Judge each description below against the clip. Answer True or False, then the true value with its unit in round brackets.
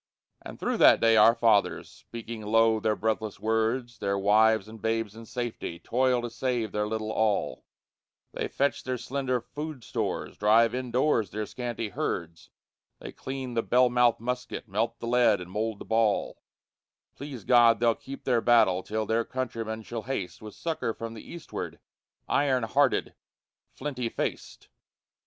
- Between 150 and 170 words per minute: True (160 wpm)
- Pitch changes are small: True (2.2 semitones)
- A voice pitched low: True (115 Hz)